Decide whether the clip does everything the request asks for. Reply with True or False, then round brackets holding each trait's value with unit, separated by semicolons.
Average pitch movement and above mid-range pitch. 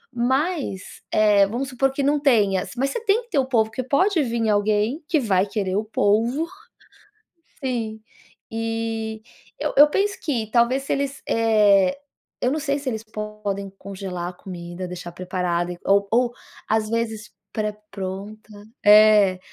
True (4.7 semitones; 220 Hz)